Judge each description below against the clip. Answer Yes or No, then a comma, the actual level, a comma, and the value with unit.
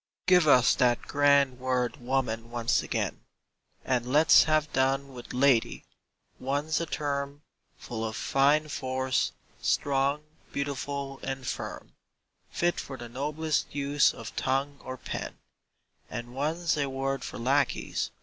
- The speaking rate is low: Yes, slow, 130 wpm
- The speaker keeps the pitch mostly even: Yes, narrow, 2.1 semitones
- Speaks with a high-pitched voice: No, low, 135 Hz